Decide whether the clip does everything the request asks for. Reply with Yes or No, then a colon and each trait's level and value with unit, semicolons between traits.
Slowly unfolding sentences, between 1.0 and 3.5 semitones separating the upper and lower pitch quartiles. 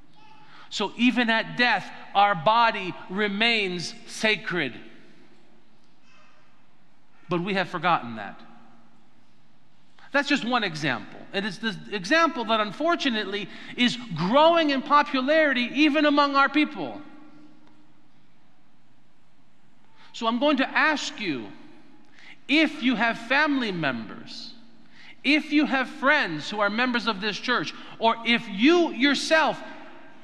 No: slow, 110 wpm; average, 5.3 semitones